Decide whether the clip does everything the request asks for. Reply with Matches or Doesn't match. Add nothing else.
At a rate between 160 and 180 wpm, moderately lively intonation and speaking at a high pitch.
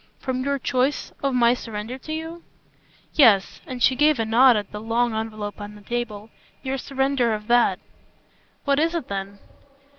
Matches